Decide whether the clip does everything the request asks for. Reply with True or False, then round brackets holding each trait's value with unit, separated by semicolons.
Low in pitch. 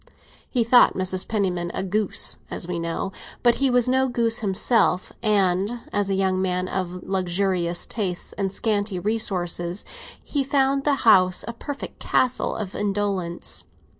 False (195 Hz)